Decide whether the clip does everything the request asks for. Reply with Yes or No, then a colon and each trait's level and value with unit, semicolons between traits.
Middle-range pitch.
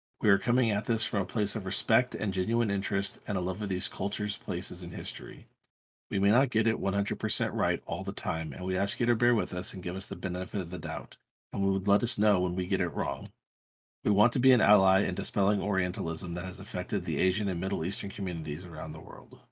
No: low, 100 Hz